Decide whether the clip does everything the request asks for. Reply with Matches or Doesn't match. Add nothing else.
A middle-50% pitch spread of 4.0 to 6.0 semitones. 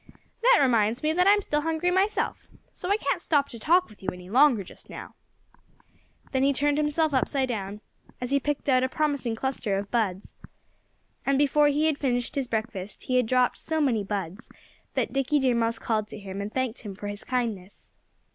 Matches